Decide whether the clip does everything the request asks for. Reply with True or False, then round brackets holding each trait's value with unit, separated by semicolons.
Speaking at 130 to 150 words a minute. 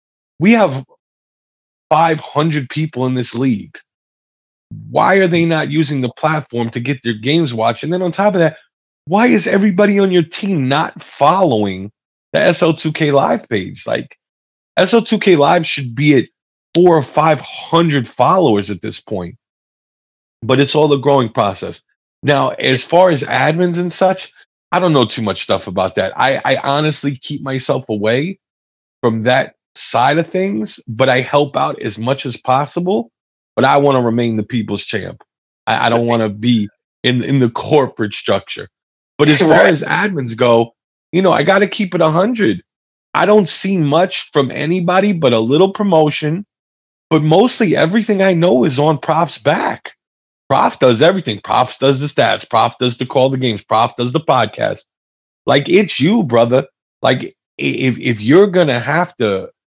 False (170 wpm)